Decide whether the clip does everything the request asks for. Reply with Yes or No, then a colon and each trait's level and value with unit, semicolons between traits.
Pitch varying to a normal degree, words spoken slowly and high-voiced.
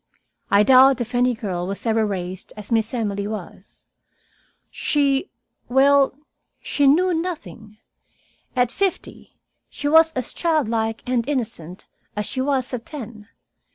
Yes: average, 4.7 semitones; slow, 130 wpm; high, 245 Hz